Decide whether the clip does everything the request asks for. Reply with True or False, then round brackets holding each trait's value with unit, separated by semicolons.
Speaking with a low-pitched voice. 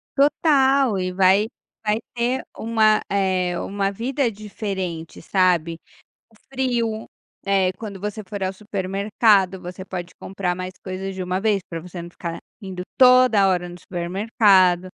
False (195 Hz)